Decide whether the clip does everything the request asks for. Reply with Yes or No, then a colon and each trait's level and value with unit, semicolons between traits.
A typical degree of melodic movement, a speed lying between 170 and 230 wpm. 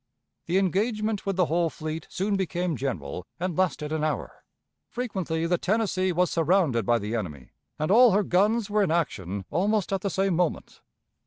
Yes: average, 4.2 semitones; average, 175 wpm